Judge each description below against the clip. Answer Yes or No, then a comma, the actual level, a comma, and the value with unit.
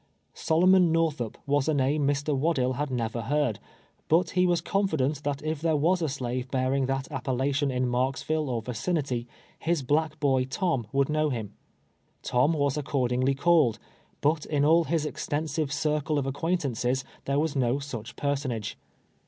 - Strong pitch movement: No, average, 3.3 semitones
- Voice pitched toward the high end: No, medium, 140 Hz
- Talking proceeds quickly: No, average, 165 wpm